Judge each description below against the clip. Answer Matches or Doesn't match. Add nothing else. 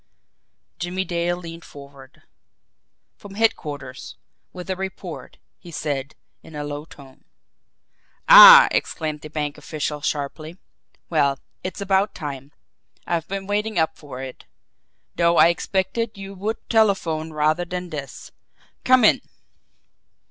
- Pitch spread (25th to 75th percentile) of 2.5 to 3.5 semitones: Doesn't match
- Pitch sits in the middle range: Matches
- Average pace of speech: Doesn't match